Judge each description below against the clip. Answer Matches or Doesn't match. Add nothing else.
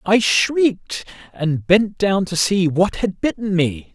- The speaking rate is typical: Matches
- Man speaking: Matches